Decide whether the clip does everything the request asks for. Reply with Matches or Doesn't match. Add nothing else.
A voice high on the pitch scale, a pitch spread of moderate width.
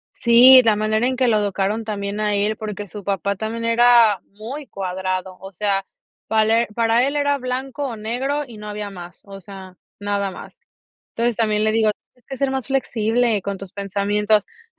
Matches